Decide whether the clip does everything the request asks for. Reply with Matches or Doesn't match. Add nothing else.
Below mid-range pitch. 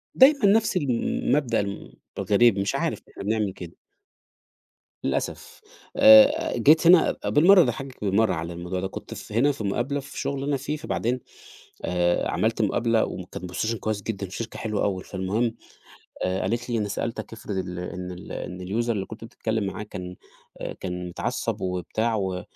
Matches